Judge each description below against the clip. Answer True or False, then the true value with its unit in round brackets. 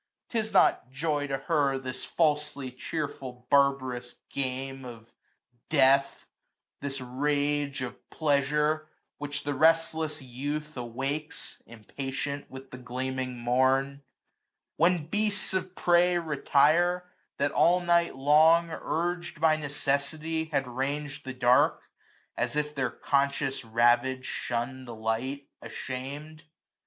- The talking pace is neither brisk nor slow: False (120 wpm)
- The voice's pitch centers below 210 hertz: True (140 Hz)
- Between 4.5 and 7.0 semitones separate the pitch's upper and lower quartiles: False (3.0 semitones)